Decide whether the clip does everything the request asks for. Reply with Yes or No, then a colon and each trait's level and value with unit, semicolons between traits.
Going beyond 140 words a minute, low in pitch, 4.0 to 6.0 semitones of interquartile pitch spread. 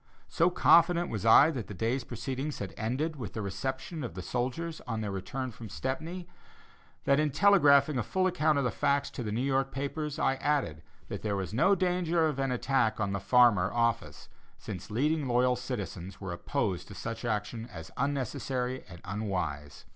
Yes: average, 185 wpm; low, 125 Hz; wide, 5.5 semitones